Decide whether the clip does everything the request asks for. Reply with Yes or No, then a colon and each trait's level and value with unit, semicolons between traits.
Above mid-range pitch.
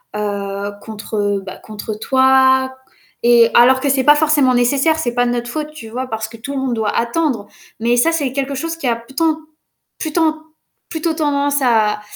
Yes: very high, 260 Hz